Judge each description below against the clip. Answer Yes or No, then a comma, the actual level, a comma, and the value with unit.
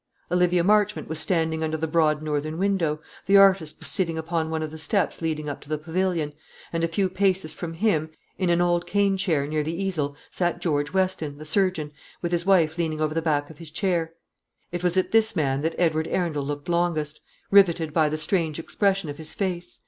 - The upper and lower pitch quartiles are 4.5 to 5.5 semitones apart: No, average, 2.9 semitones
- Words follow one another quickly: Yes, fast, 210 wpm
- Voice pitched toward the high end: No, medium, 165 Hz